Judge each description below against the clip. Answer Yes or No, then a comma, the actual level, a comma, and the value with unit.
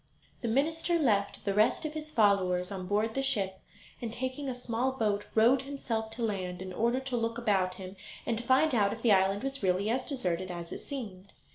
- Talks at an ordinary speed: No, fast, 215 wpm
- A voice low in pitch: No, high, 225 Hz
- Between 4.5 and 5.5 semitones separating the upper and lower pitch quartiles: Yes, average, 5.1 semitones